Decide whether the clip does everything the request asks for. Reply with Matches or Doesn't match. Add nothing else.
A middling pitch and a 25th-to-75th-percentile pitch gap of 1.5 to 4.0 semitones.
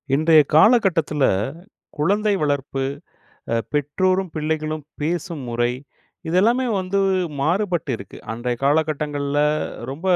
Doesn't match